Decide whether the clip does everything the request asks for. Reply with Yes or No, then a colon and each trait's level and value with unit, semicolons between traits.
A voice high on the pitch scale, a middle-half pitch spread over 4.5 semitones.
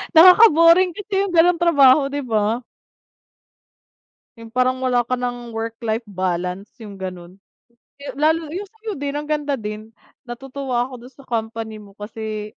Yes: very high, 250 Hz; wide, 5.4 semitones